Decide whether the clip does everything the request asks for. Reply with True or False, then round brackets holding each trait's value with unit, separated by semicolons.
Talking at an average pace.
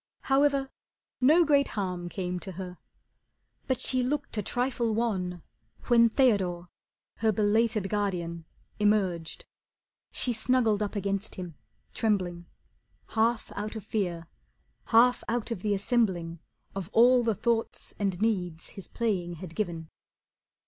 False (130 wpm)